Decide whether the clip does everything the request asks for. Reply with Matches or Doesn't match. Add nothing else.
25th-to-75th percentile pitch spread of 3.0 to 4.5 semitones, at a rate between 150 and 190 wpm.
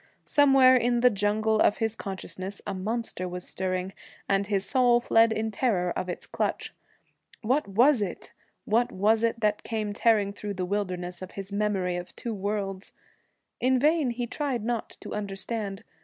Matches